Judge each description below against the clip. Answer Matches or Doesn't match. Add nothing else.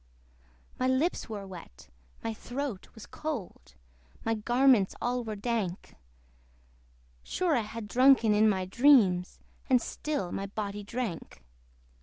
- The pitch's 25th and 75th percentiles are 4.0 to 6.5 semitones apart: Matches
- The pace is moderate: Doesn't match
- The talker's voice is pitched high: Matches